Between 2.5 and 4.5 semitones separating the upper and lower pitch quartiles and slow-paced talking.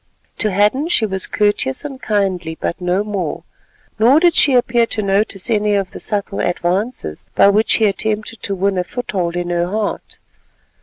No: average, 3.1 semitones; average, 175 wpm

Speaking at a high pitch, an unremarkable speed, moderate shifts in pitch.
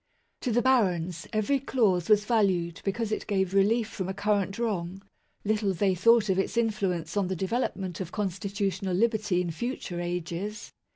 Yes: high, 195 Hz; average, 165 wpm; average, 3.2 semitones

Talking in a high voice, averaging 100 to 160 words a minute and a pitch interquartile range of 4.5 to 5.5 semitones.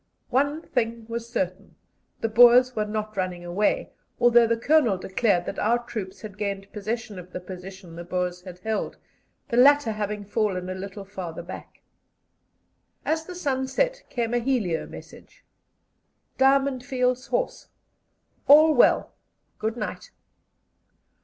Yes: high, 220 Hz; average, 140 wpm; average, 4.8 semitones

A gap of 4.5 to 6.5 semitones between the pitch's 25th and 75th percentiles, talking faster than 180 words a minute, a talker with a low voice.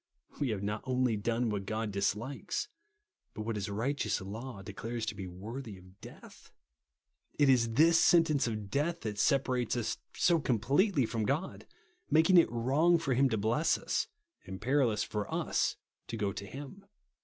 No: average, 4.9 semitones; average, 175 wpm; low, 115 Hz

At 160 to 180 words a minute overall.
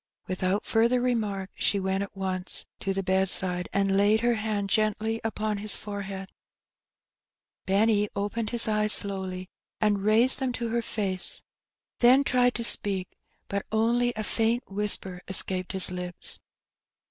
No: average, 145 wpm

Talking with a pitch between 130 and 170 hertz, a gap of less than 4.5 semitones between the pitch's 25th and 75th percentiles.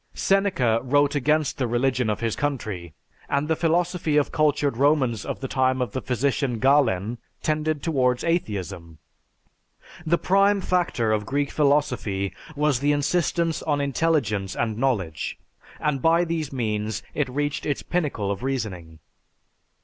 No: low, 135 Hz; average, 5.1 semitones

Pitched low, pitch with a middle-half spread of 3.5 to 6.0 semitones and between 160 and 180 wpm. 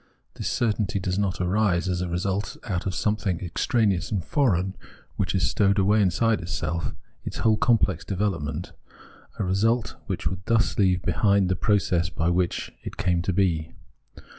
No: very low, 95 Hz; average, 2.8 semitones; average, 165 wpm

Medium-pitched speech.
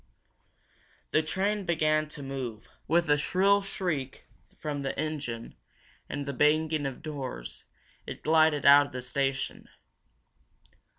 Yes: medium, 150 Hz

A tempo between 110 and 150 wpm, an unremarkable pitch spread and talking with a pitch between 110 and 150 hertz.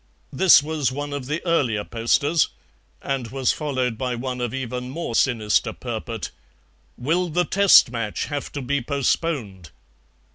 Yes: average, 145 wpm; average, 3.7 semitones; low, 135 Hz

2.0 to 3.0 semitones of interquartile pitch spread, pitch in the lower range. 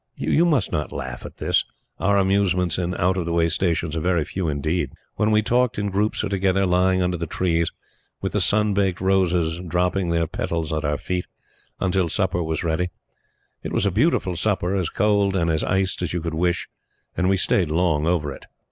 Yes: average, 2.7 semitones; very low, 90 Hz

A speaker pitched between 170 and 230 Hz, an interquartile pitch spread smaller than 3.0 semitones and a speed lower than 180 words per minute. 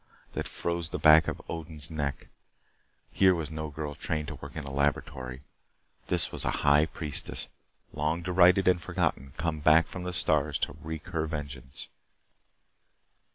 No: very low, 80 Hz; narrow, 2.6 semitones; average, 155 wpm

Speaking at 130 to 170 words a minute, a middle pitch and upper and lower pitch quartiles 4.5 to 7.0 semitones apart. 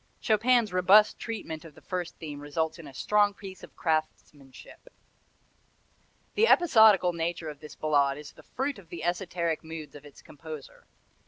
Yes: average, 160 wpm; medium, 170 Hz; average, 5.0 semitones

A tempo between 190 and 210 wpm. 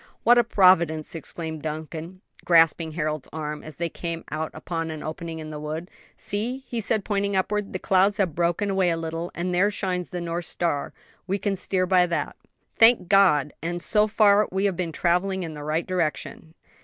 Yes: average, 195 wpm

